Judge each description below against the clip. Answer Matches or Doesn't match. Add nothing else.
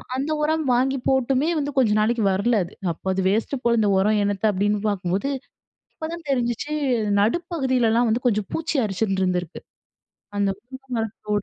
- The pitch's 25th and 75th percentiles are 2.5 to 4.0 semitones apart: Doesn't match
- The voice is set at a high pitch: Matches